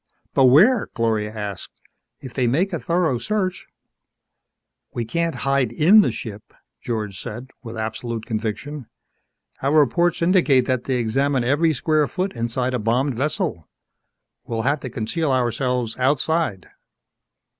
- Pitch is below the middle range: Yes, low, 130 Hz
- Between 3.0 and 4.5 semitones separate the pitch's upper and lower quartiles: No, average, 5.2 semitones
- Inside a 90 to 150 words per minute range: Yes, average, 140 wpm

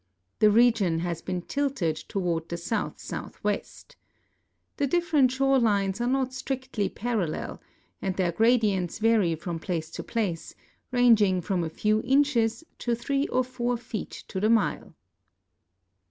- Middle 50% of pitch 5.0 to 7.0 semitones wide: Yes, wide, 5.5 semitones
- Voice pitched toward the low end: No, high, 220 Hz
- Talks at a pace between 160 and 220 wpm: No, average, 145 wpm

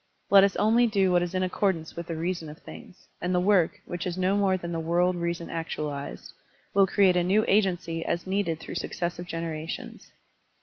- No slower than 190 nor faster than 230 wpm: Yes, average, 200 wpm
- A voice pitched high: No, medium, 180 Hz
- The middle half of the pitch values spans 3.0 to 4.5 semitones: No, narrow, 2.4 semitones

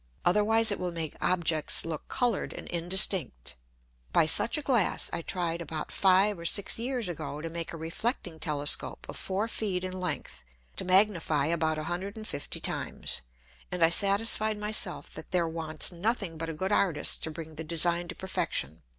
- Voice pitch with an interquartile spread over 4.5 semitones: No, average, 3.8 semitones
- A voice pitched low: No, medium, 175 Hz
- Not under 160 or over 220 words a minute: Yes, average, 175 wpm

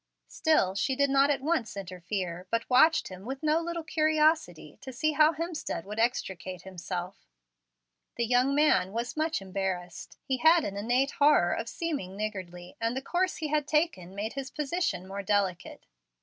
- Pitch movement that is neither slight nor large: No, wide, 8.2 semitones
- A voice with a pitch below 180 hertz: No, high, 240 Hz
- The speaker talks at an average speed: Yes, average, 165 wpm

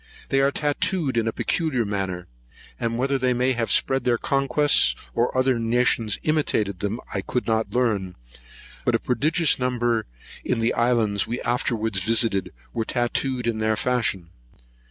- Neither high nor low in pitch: No, low, 120 Hz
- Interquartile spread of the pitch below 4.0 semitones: Yes, average, 2.8 semitones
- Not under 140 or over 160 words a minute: Yes, average, 155 wpm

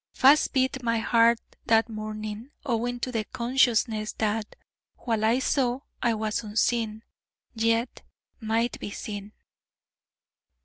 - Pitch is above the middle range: Yes, high, 230 Hz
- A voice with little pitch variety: Yes, narrow, 2.0 semitones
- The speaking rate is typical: No, slow, 120 wpm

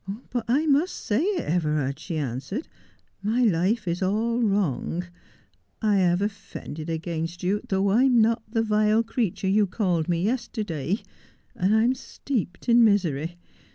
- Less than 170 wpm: Yes, average, 160 wpm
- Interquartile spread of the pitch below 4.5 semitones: No, average, 5.0 semitones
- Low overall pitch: No, high, 205 Hz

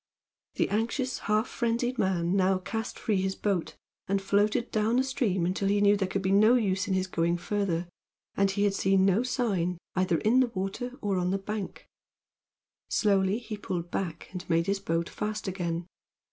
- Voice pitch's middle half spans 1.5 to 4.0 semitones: Yes, narrow, 2.6 semitones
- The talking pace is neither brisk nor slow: Yes, average, 190 wpm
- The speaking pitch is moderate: No, high, 195 Hz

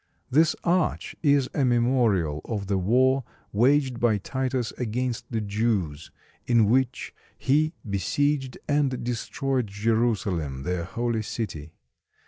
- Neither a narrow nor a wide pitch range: Yes, average, 4.4 semitones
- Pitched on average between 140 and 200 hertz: No, low, 120 Hz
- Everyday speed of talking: No, slow, 115 wpm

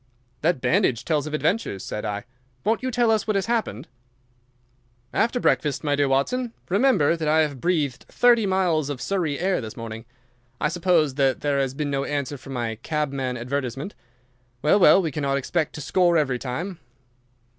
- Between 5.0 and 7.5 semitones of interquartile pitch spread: Yes, average, 5.3 semitones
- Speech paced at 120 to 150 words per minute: No, average, 175 wpm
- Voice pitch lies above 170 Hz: No, medium, 150 Hz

